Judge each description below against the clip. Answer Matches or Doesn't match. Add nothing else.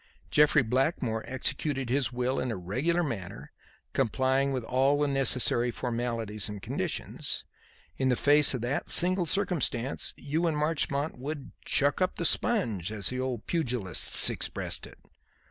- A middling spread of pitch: Matches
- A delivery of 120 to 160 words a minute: Matches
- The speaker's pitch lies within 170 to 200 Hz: Doesn't match